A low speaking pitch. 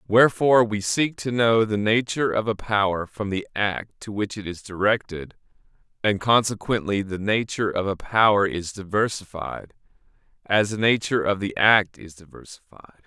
Yes: low, 105 Hz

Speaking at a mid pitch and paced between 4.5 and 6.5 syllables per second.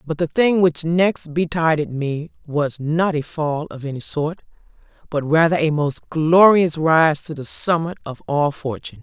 No: medium, 155 Hz; 4.2 syllables/s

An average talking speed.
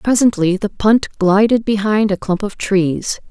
Yes: average, 165 wpm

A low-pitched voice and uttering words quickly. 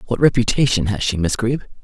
No: low, 110 Hz; average, 195 wpm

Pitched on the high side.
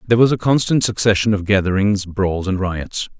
No: low, 100 Hz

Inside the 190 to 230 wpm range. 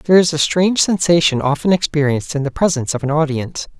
Yes: fast, 205 wpm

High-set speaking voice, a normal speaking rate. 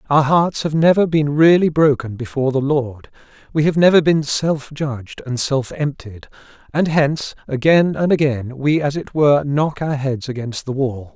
No: medium, 145 Hz; average, 185 wpm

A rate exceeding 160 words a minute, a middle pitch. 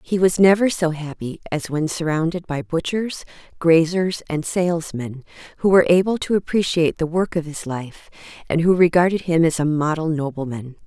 Yes: average, 170 wpm; medium, 165 Hz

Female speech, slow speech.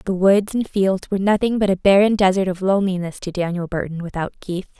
No: female; average, 200 wpm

